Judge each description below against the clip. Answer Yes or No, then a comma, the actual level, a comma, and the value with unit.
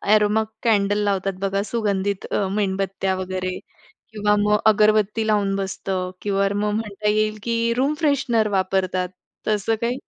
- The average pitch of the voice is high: Yes, high, 205 Hz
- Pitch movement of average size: No, narrow, 1.8 semitones